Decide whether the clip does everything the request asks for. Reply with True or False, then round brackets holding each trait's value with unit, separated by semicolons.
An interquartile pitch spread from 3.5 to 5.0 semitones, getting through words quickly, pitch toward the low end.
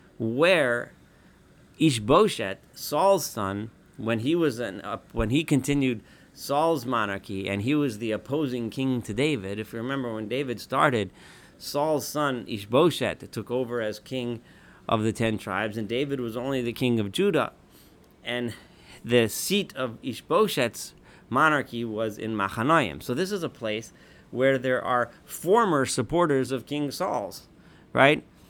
False (4.3 semitones; 145 wpm; 120 Hz)